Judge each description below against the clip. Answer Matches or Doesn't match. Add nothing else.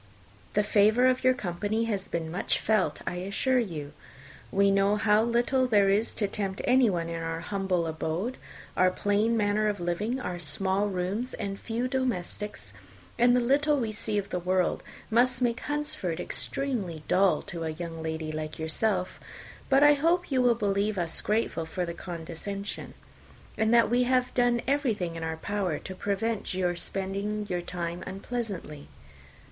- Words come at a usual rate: Matches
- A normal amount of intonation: Matches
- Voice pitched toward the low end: Doesn't match